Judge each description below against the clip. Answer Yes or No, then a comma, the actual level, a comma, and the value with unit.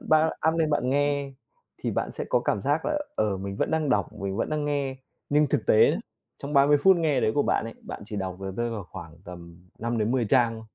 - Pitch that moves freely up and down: Yes, wide, 6.4 semitones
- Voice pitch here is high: No, low, 125 Hz